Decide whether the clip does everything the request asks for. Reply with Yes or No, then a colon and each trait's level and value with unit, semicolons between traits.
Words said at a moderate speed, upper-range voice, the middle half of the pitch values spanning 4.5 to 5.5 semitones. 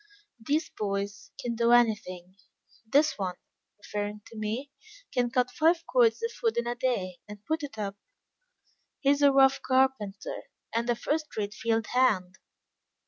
Yes: average, 155 wpm; high, 235 Hz; average, 4.9 semitones